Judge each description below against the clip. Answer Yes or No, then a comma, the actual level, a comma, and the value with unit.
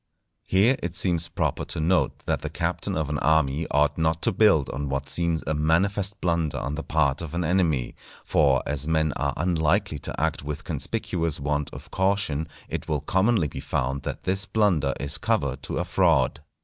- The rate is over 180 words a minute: Yes, average, 190 wpm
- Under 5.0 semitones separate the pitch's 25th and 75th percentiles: Yes, average, 3.6 semitones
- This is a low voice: Yes, very low, 80 Hz